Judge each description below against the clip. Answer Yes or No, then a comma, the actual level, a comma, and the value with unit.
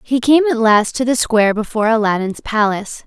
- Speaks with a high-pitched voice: Yes, high, 225 Hz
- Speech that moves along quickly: No, average, 195 wpm